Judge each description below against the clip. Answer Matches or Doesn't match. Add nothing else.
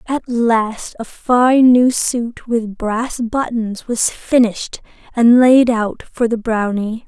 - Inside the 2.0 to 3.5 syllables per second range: Matches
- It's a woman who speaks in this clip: Matches